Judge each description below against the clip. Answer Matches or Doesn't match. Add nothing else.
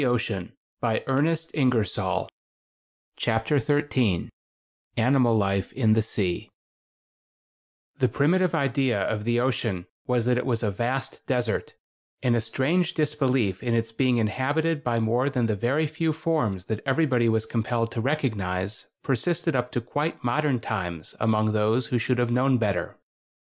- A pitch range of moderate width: Matches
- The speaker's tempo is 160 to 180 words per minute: Doesn't match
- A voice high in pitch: Doesn't match